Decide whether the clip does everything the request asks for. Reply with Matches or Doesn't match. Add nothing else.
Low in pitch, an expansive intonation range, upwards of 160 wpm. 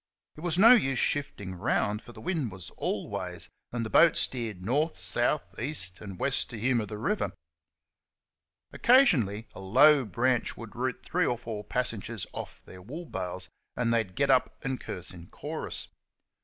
Matches